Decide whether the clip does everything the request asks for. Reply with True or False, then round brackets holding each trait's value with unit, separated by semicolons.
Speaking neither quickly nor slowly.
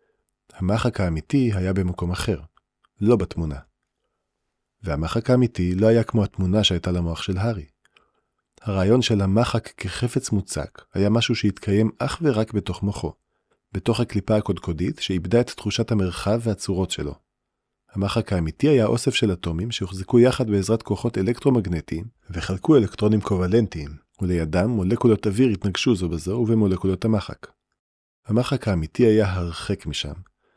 True (130 wpm)